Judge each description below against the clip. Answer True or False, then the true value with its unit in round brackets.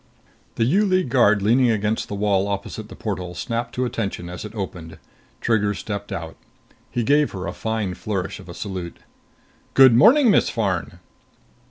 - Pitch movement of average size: True (3.7 semitones)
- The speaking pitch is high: False (105 Hz)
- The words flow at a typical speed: True (170 wpm)